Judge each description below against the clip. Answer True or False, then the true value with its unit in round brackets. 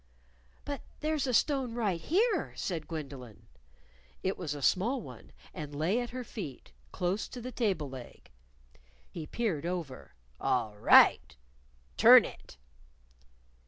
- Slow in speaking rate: True (130 wpm)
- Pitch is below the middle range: False (180 Hz)